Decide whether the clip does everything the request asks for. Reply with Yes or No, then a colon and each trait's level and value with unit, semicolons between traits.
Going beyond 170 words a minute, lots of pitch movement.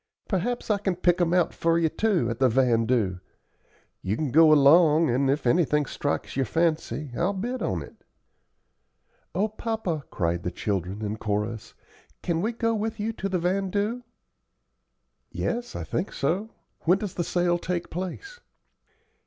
No: average, 160 wpm; wide, 6.8 semitones